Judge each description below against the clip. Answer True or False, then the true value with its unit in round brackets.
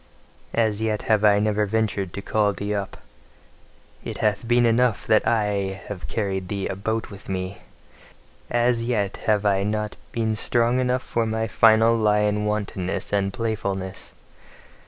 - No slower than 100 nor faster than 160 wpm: True (150 wpm)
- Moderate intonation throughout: False (2.1 semitones)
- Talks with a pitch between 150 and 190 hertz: False (105 Hz)